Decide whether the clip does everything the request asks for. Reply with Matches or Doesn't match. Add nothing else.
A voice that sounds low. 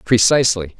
Matches